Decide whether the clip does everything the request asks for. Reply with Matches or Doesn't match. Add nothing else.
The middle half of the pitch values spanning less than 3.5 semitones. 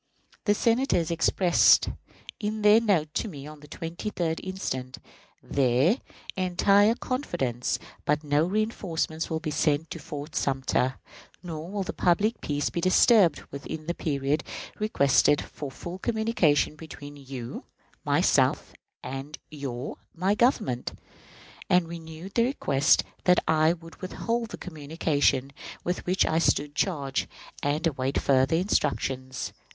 Doesn't match